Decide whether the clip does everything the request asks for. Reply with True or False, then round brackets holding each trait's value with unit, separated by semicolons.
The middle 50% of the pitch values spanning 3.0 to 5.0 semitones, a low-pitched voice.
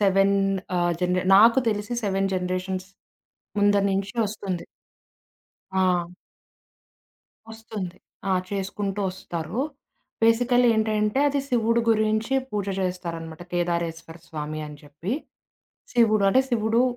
False (3.4 semitones; 195 Hz)